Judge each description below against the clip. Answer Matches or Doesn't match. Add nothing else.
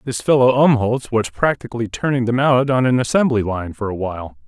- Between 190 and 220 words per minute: Matches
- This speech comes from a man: Matches